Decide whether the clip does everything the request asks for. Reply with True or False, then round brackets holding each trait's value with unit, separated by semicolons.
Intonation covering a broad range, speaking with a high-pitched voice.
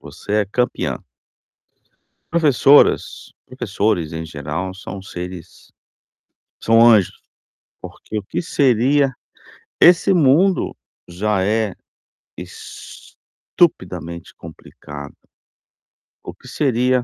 False (7.0 semitones; 105 Hz)